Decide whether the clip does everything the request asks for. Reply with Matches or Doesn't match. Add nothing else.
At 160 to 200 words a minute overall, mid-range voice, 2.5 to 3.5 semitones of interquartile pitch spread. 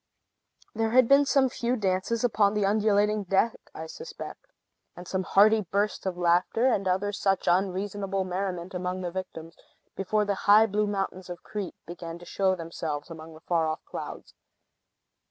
Doesn't match